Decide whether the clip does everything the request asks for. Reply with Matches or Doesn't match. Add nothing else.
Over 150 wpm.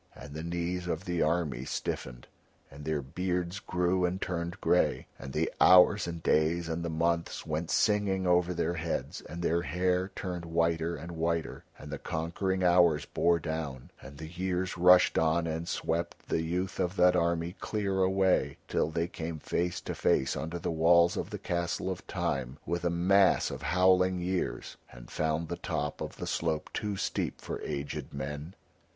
Matches